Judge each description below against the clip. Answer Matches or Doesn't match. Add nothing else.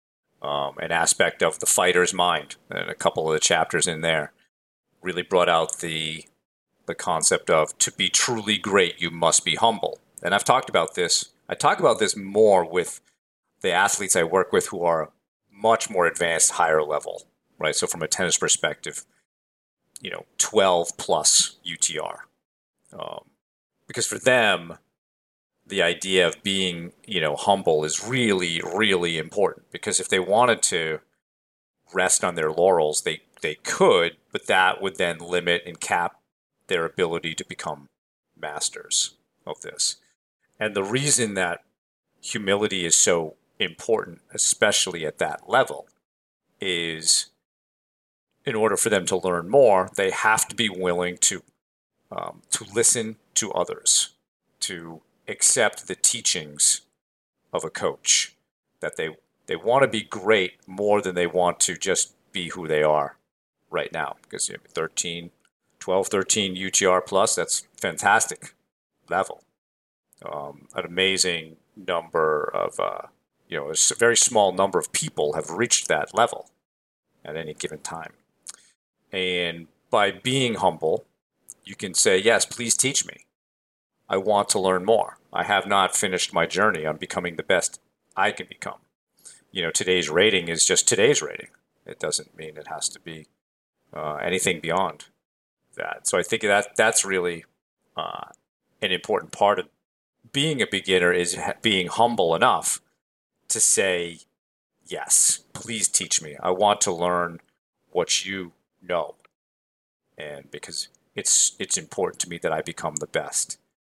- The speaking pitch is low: Matches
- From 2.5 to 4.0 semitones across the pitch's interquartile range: Doesn't match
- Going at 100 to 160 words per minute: Matches